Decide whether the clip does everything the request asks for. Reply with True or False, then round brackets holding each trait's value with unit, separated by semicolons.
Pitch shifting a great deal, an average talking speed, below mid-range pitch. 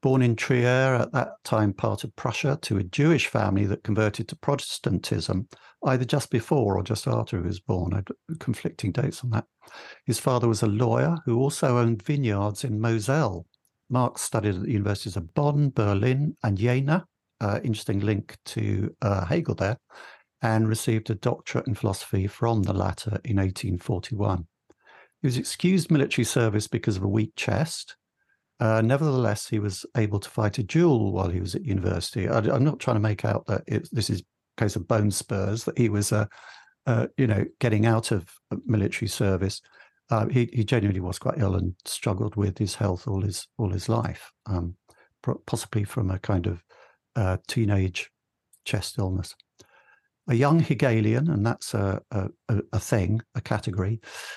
False (3.8 semitones; 180 wpm; 110 Hz)